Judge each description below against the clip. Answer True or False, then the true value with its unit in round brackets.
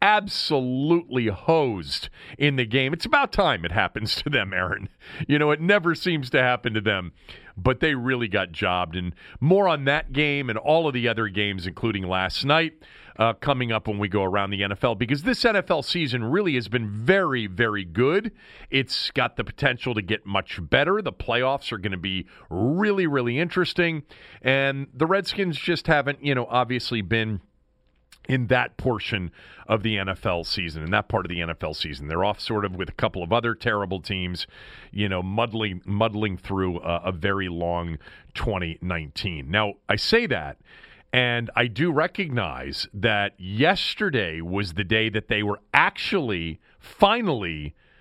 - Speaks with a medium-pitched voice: False (115 Hz)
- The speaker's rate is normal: True (175 wpm)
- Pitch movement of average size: False (6.2 semitones)